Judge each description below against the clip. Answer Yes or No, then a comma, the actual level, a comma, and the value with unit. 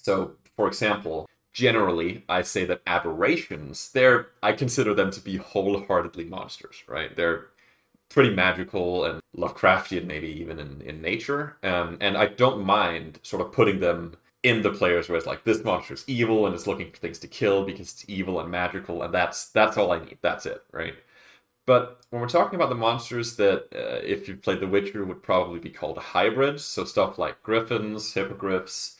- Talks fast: No, average, 190 wpm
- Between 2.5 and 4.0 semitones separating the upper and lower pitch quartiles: No, average, 5.1 semitones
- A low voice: Yes, low, 100 Hz